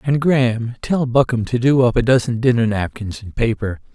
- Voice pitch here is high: No, low, 120 Hz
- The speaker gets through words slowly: No, average, 200 wpm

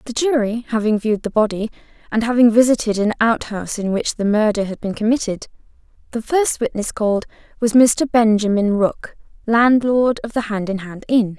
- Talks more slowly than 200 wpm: Yes, average, 175 wpm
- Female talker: Yes, female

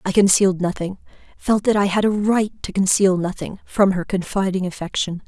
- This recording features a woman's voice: Yes, female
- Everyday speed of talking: Yes, average, 160 wpm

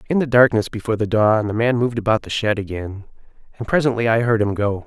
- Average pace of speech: No, fast, 235 wpm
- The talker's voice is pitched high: No, low, 110 Hz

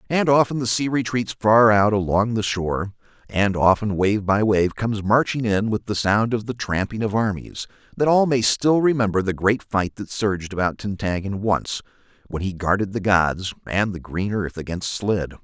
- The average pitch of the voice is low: Yes, low, 105 Hz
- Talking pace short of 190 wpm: No, average, 195 wpm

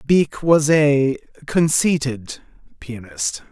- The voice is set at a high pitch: No, medium, 140 Hz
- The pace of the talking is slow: Yes, slow, 85 wpm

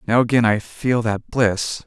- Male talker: Yes, male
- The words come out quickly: No, average, 195 wpm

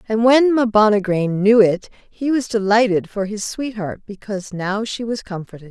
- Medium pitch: No, high, 210 Hz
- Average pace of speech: Yes, average, 170 wpm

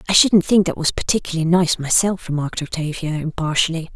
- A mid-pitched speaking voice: Yes, medium, 170 Hz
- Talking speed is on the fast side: No, average, 165 wpm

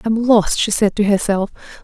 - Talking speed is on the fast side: Yes, fast, 230 wpm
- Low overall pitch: No, high, 210 Hz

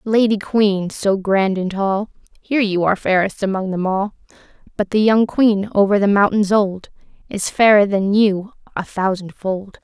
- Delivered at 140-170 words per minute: Yes, average, 165 wpm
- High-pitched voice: Yes, high, 200 Hz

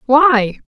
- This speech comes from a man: No, female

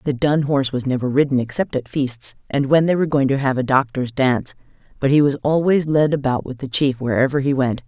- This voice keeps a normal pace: No, fast, 235 wpm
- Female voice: Yes, female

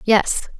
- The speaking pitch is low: No, high, 210 Hz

